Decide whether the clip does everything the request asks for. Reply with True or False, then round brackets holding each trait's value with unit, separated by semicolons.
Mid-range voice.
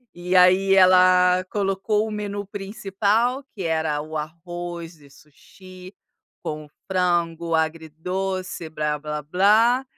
True (180 Hz)